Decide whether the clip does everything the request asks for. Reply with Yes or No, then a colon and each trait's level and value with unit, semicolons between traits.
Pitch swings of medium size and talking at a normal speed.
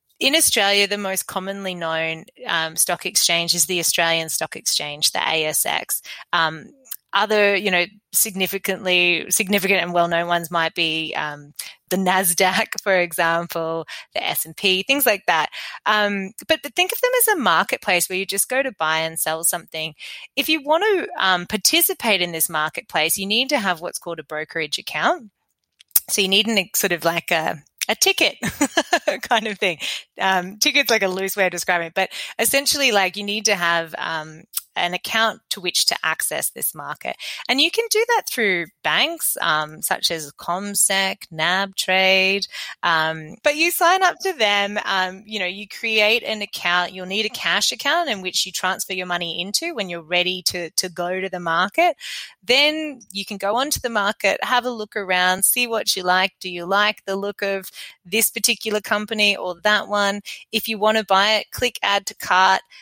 Yes: average, 4.0 semitones; average, 190 wpm